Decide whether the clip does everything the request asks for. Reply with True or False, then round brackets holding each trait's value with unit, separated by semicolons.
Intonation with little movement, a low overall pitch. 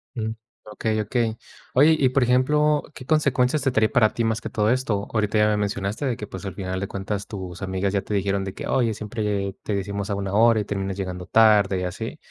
False (3.1 semitones; 105 Hz)